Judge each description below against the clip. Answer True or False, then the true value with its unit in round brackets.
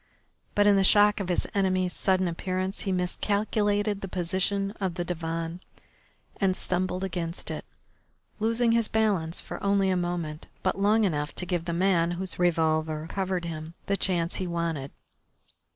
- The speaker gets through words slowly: False (160 wpm)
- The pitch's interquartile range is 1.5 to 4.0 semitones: True (2.8 semitones)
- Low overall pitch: False (185 Hz)